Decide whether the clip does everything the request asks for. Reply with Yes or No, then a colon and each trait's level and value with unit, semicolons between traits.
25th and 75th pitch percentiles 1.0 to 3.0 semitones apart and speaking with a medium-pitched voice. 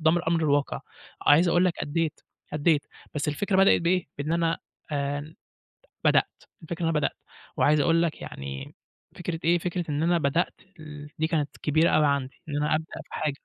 Yes: narrow, 2.6 semitones; medium, 155 Hz